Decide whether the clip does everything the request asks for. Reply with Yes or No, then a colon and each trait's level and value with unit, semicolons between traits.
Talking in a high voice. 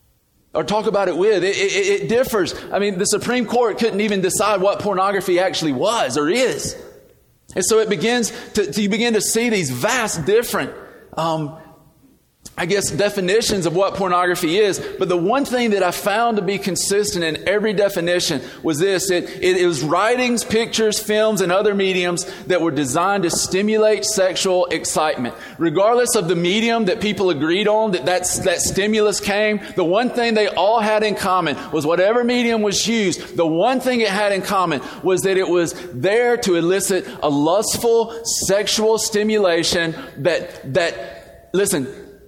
Yes: high, 200 Hz